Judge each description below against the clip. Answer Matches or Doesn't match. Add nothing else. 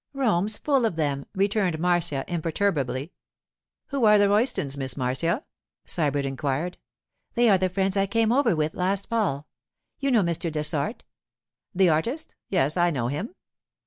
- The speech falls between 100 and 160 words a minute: Matches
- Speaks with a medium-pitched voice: Matches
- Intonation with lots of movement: Matches